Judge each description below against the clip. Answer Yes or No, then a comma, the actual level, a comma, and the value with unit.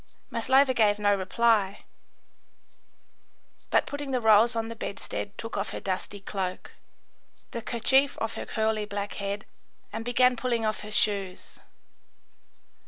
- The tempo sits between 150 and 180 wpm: No, slow, 135 wpm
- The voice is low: No, high, 220 Hz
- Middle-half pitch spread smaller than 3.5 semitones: Yes, narrow, 2.6 semitones